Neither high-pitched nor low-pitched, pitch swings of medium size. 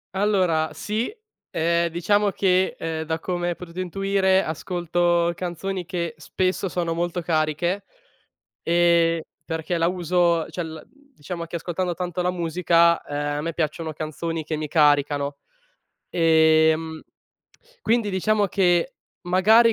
No: medium, 170 Hz; narrow, 2.3 semitones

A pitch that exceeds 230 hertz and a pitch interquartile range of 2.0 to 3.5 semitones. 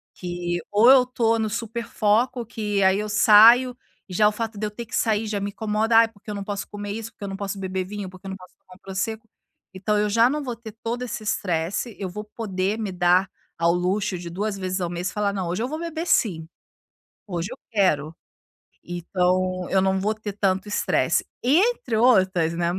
No: high, 205 Hz; average, 3.2 semitones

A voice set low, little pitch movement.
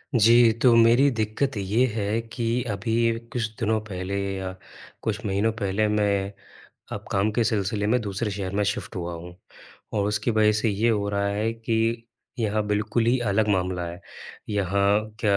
Yes: low, 105 Hz; narrow, 2.3 semitones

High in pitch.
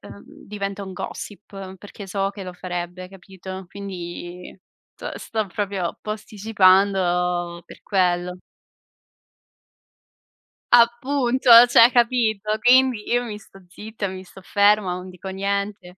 Yes: high, 195 Hz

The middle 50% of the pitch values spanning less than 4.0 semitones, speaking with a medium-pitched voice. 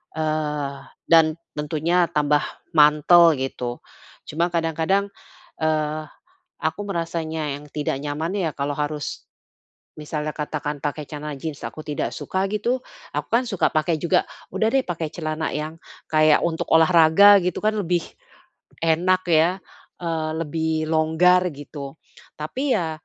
Yes: narrow, 2.5 semitones; medium, 160 Hz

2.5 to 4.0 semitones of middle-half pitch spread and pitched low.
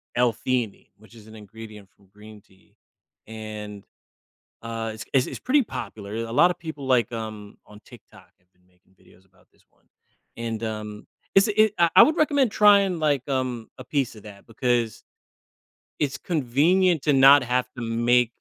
No: average, 4.8 semitones; low, 115 Hz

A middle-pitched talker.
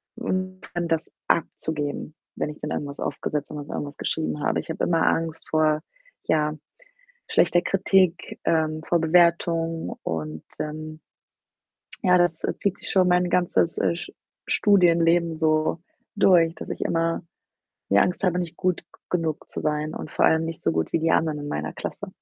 Yes: medium, 165 Hz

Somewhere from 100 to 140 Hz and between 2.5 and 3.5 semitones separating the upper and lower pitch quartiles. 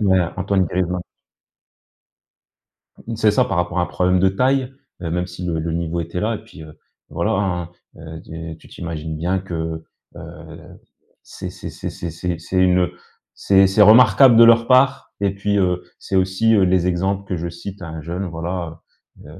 No: very low, 90 Hz; average, 2.9 semitones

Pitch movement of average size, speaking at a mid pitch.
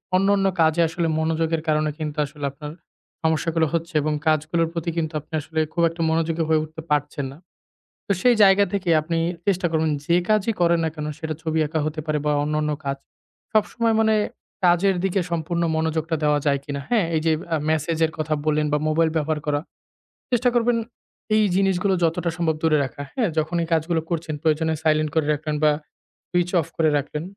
No: narrow, 2.1 semitones; medium, 160 Hz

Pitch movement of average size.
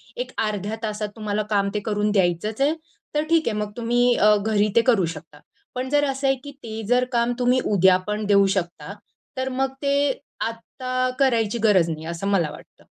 Yes: average, 4.1 semitones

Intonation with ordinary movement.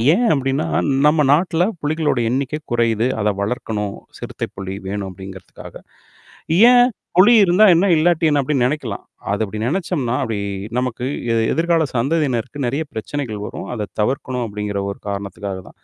No: wide, 6.9 semitones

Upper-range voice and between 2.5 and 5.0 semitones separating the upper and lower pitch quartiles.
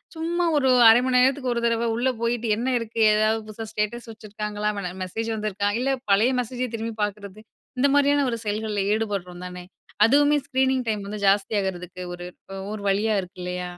Yes: high, 220 Hz; average, 3.6 semitones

